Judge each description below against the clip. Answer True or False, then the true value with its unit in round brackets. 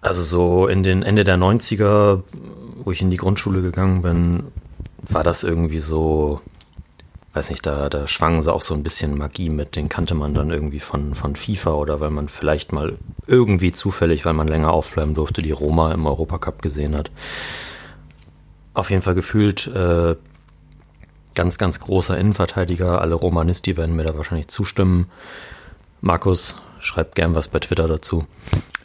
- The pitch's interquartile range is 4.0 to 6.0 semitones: False (3.2 semitones)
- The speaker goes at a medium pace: True (165 wpm)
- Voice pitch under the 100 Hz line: True (85 Hz)